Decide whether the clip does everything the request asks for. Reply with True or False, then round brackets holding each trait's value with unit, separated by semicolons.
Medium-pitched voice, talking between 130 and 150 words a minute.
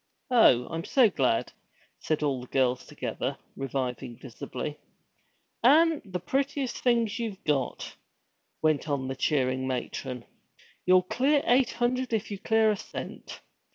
True (180 Hz; 135 wpm)